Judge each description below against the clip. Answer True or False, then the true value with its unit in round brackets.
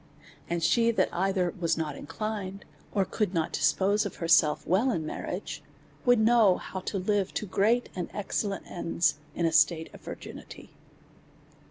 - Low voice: False (190 Hz)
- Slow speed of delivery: False (165 wpm)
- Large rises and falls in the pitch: False (4.0 semitones)